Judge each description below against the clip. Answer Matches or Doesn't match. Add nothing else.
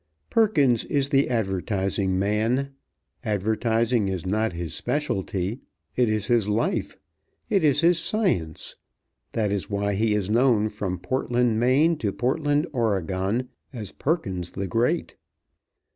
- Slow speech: Matches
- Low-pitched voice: Matches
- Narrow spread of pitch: Doesn't match